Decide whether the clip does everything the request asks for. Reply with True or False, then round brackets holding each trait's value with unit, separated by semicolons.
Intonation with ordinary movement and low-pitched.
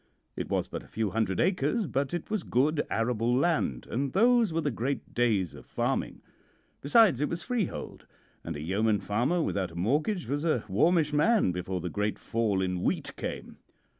False (8.4 semitones; 130 Hz)